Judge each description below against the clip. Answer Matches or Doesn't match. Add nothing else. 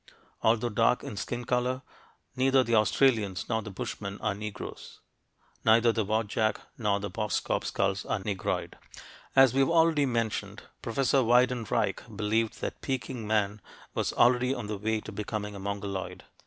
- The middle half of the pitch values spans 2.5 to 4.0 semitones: Matches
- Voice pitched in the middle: Doesn't match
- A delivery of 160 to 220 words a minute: Doesn't match